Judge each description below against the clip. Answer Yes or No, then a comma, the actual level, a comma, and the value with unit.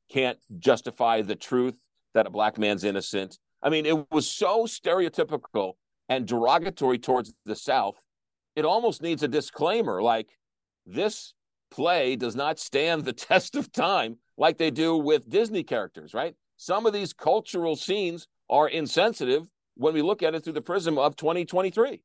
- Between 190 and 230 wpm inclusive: No, average, 160 wpm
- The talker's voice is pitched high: No, medium, 155 Hz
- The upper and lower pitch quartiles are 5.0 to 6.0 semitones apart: Yes, wide, 5.6 semitones